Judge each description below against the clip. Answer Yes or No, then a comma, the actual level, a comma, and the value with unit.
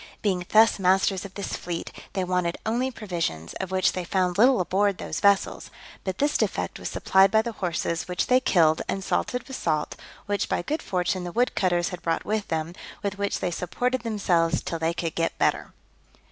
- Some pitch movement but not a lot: Yes, average, 3.2 semitones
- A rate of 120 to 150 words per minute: No, average, 200 wpm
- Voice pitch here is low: No, medium, 185 Hz